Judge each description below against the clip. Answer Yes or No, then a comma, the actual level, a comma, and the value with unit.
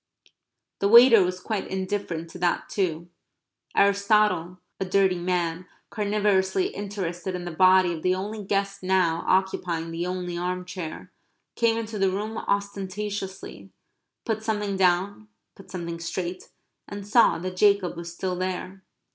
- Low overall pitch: No, high, 190 Hz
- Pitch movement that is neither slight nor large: No, narrow, 2.2 semitones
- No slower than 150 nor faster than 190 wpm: No, average, 140 wpm